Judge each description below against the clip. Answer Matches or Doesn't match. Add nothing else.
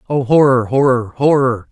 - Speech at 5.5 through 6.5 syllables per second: Doesn't match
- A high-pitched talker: Doesn't match